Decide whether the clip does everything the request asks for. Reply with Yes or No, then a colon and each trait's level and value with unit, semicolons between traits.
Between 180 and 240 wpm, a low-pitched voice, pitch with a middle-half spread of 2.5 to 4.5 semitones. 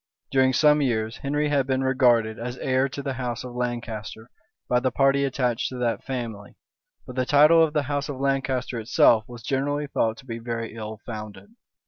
Yes: average, 190 wpm; low, 130 Hz; average, 3.0 semitones